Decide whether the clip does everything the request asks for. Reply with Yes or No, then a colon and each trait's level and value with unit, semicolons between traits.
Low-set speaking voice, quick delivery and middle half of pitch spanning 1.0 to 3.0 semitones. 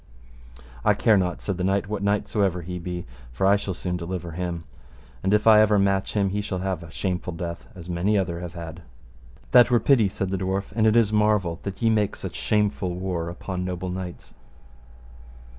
Yes: very low, 95 Hz; fast, 210 wpm; average, 2.7 semitones